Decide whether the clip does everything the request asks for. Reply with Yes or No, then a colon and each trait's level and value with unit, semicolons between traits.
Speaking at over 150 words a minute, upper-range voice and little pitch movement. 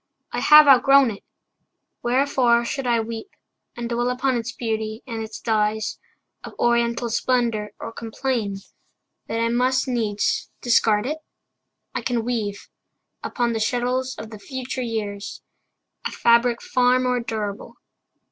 No: average, 140 wpm; high, 235 Hz; narrow, 2.2 semitones